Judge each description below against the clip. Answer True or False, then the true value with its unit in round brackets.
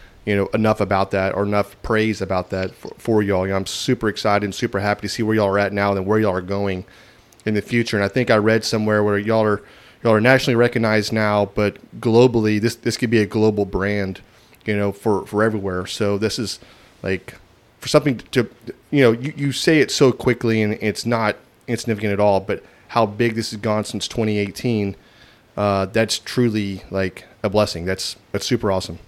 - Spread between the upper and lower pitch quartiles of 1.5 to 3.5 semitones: True (2.4 semitones)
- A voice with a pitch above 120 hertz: False (105 Hz)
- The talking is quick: True (215 wpm)